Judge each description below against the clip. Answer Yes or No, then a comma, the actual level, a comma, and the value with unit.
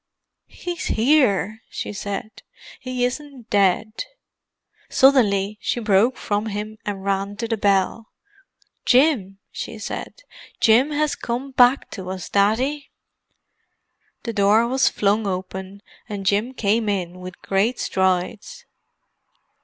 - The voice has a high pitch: Yes, high, 215 Hz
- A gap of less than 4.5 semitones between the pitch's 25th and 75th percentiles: Yes, average, 4.1 semitones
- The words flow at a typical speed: No, slow, 120 wpm